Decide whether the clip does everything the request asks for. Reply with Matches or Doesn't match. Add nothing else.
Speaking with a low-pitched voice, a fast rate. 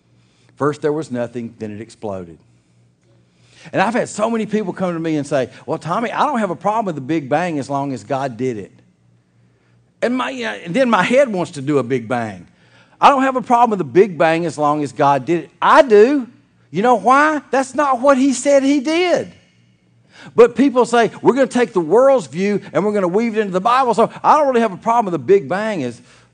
Doesn't match